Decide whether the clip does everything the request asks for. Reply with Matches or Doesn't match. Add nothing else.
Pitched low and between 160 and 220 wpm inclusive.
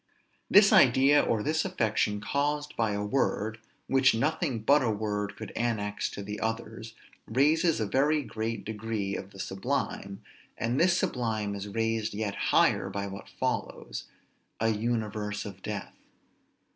Doesn't match